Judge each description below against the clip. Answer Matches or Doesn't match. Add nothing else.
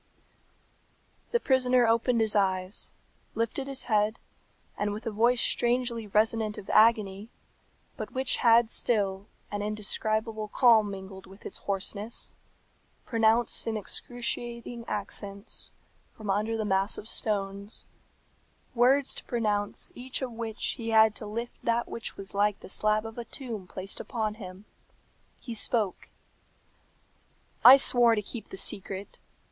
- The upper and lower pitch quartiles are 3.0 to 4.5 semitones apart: Doesn't match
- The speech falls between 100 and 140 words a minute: Matches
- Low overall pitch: Doesn't match